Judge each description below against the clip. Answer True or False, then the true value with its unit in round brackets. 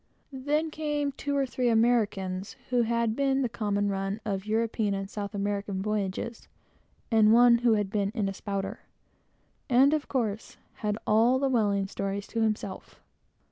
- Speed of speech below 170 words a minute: True (160 wpm)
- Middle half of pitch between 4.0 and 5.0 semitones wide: False (3.5 semitones)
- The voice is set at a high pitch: True (220 Hz)